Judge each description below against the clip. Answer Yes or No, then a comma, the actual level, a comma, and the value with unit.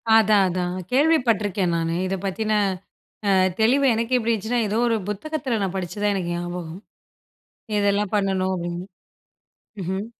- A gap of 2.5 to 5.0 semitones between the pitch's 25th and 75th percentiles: Yes, average, 3.8 semitones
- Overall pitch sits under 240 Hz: Yes, high, 200 Hz